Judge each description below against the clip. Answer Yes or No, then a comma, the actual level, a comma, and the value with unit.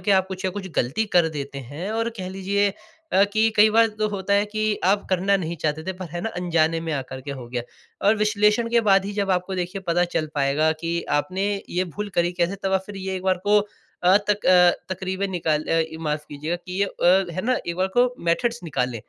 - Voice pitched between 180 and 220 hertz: Yes, medium, 185 Hz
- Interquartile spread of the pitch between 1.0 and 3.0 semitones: No, average, 3.5 semitones